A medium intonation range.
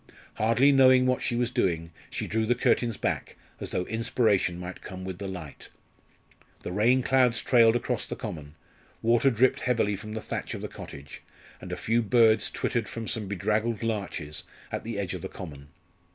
Yes: average, 4.2 semitones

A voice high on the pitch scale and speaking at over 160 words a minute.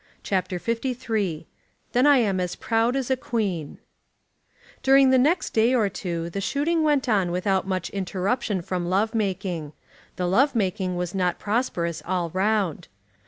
No: high, 200 Hz; average, 155 wpm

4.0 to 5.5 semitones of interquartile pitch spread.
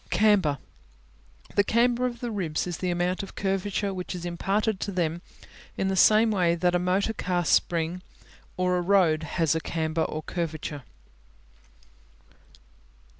No: average, 3.0 semitones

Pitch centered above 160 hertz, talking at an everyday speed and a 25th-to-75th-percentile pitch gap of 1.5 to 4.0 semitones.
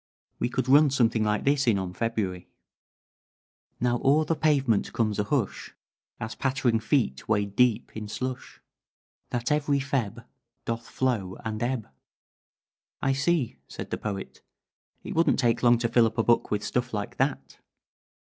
No: low, 120 Hz; average, 155 wpm; average, 3.7 semitones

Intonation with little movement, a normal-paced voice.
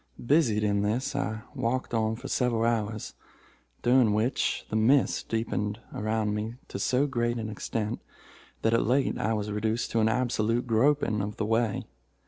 Yes: narrow, 2.2 semitones; average, 165 wpm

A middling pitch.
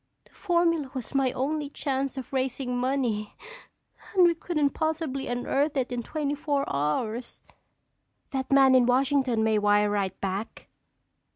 No: very high, 265 Hz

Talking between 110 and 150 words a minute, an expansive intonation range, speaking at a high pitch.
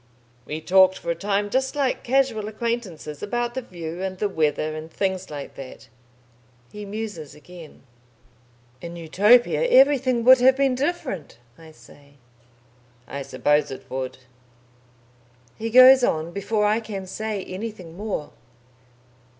Yes: slow, 135 wpm; wide, 6.8 semitones; high, 200 Hz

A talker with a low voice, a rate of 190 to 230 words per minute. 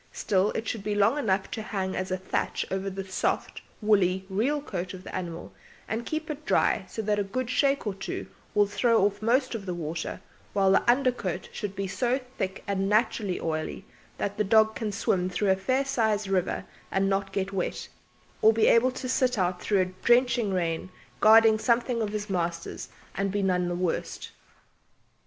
No: high, 200 Hz; average, 195 wpm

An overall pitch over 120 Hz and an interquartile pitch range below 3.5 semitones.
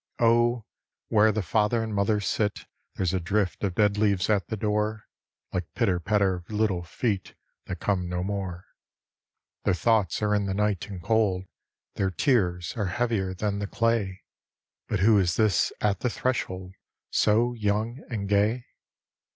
No: low, 105 Hz; average, 2.7 semitones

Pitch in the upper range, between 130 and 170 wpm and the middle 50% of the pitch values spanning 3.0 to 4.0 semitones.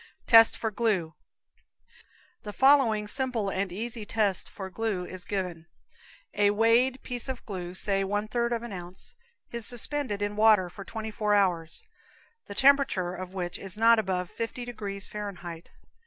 Yes: high, 210 Hz; average, 155 wpm; average, 3.6 semitones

